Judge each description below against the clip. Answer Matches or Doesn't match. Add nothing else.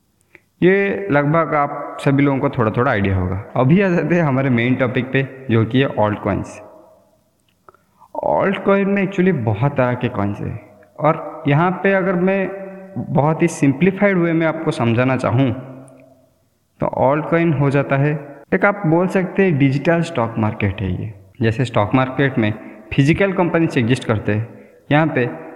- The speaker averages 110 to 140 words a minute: Doesn't match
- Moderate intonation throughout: Doesn't match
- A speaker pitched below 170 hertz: Matches